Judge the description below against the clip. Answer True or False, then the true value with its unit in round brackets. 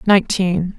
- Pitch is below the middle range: False (185 Hz)